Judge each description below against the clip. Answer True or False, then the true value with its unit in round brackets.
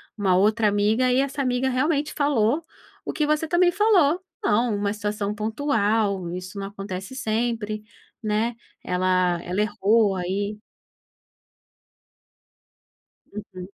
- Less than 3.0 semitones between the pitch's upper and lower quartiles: False (4.6 semitones)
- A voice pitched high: True (215 Hz)